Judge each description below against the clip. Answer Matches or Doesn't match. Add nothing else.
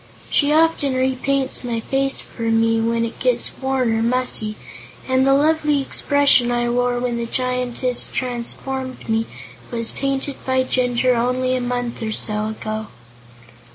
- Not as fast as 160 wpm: Matches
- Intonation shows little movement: Matches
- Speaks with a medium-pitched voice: Doesn't match